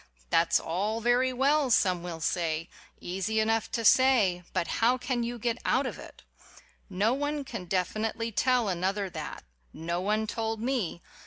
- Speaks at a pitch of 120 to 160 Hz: No, high, 220 Hz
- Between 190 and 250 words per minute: No, average, 160 wpm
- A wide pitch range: No, average, 5.0 semitones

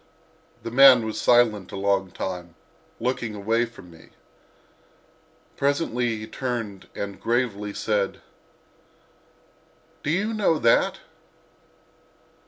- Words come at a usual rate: No, slow, 100 wpm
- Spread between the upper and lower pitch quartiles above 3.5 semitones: Yes, average, 3.9 semitones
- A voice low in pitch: Yes, low, 115 Hz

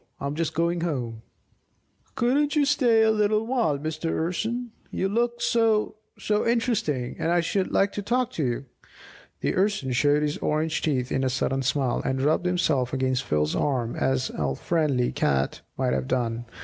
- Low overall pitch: No, medium, 155 Hz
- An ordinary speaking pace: Yes, average, 175 wpm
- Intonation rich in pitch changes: Yes, wide, 8.5 semitones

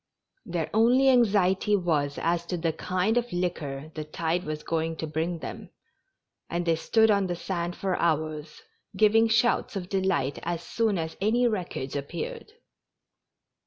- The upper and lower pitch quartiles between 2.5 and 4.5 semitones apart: No, average, 4.9 semitones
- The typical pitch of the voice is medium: Yes, medium, 175 Hz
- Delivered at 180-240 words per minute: No, average, 155 wpm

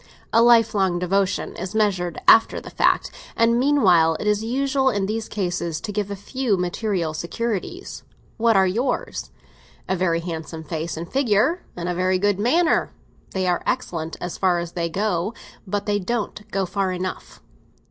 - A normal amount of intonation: Yes, average, 4.2 semitones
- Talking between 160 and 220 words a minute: Yes, average, 170 wpm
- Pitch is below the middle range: No, high, 195 Hz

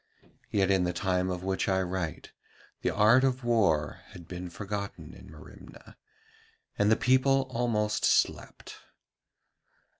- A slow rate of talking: Yes, slow, 130 wpm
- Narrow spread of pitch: No, average, 4.2 semitones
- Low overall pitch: Yes, low, 100 Hz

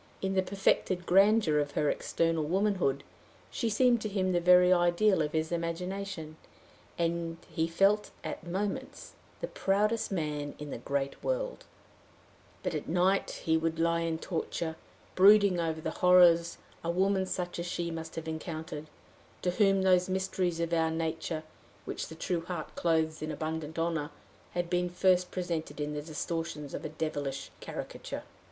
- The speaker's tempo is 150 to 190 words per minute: Yes, average, 160 wpm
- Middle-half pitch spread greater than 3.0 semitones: No, average, 2.7 semitones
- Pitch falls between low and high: Yes, medium, 170 Hz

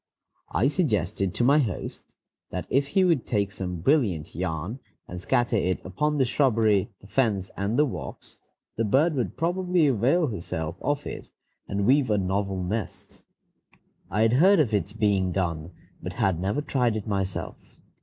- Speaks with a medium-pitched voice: No, low, 110 Hz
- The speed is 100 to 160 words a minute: No, average, 170 wpm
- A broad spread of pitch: Yes, wide, 6.5 semitones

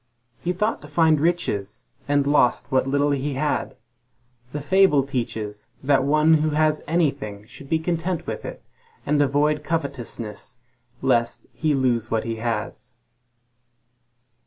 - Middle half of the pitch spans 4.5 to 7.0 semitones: No, average, 4.1 semitones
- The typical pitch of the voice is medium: Yes, medium, 145 Hz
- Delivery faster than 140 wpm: No, slow, 135 wpm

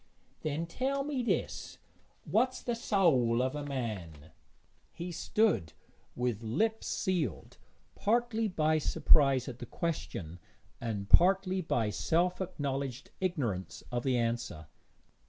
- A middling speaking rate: No, slow, 120 wpm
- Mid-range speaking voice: Yes, medium, 145 Hz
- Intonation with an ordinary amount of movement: No, wide, 8.2 semitones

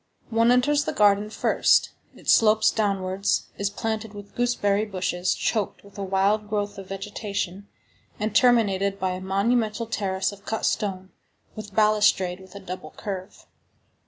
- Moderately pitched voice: No, high, 205 Hz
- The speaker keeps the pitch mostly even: Yes, narrow, 2.1 semitones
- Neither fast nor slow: Yes, average, 150 wpm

